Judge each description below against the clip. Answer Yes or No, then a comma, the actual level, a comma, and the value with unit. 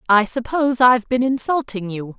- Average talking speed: Yes, average, 165 wpm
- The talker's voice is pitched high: Yes, high, 240 Hz